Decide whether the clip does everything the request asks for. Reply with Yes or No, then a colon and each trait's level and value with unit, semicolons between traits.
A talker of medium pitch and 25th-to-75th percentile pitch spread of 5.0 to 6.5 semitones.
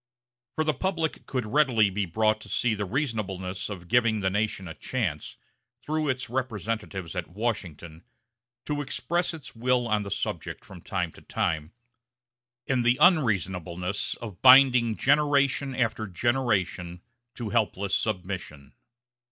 No: low, 110 Hz; wide, 5.4 semitones